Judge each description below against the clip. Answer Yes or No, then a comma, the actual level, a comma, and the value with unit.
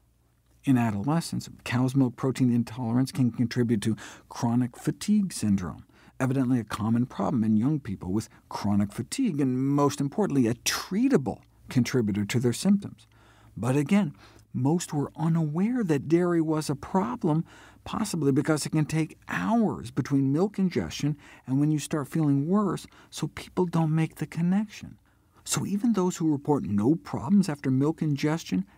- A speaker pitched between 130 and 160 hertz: Yes, medium, 140 Hz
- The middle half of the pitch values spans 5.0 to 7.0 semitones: Yes, wide, 5.5 semitones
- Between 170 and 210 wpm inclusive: No, average, 150 wpm